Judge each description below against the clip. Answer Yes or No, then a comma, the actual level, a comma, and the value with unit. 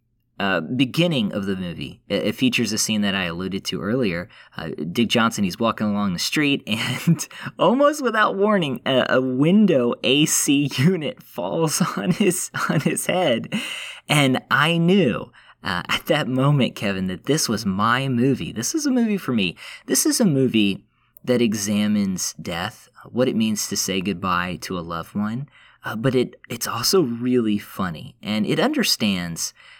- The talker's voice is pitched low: Yes, low, 125 Hz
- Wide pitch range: Yes, wide, 7.2 semitones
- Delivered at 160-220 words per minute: Yes, average, 170 wpm